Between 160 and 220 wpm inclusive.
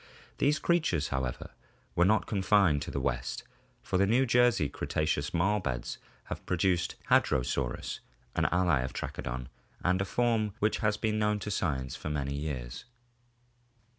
No: average, 150 wpm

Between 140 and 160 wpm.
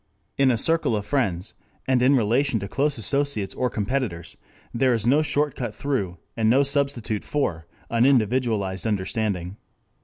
Yes: average, 150 wpm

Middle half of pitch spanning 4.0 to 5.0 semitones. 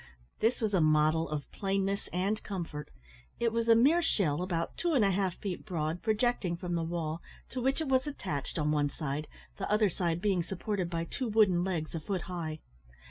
Yes: average, 4.7 semitones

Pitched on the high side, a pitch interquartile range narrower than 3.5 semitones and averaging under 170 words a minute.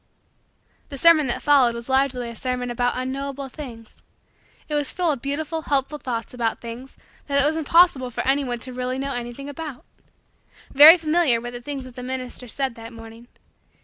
No: very high, 260 Hz; average, 2.9 semitones; average, 180 wpm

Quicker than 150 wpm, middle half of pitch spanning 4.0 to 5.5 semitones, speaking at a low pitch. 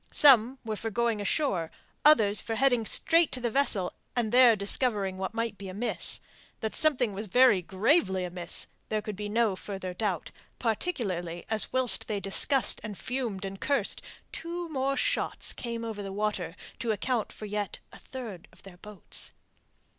No: average, 170 wpm; average, 4.4 semitones; high, 215 Hz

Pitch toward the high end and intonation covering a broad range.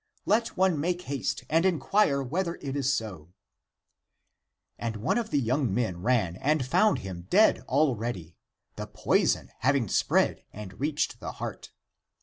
No: low, 135 Hz; wide, 7.0 semitones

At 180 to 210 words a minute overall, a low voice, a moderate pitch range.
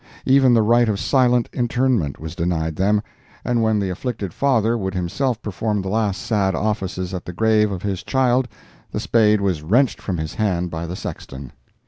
Yes: average, 185 wpm; low, 105 Hz; average, 4.4 semitones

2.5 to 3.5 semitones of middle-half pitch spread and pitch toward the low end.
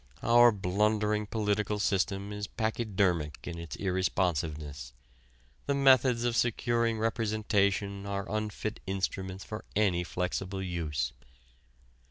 Yes: average, 2.9 semitones; low, 100 Hz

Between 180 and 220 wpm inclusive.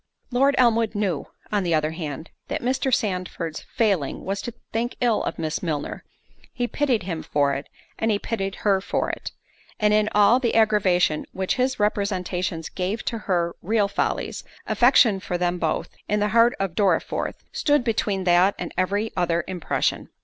No: average, 165 wpm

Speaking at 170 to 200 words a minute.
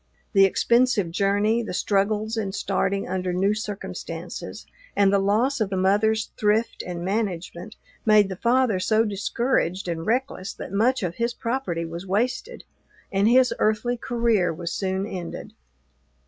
No: average, 145 wpm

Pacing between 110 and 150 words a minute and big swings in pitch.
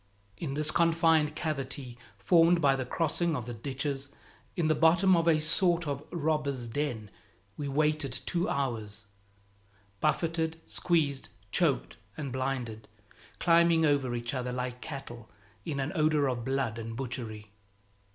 No: average, 140 wpm; average, 4.4 semitones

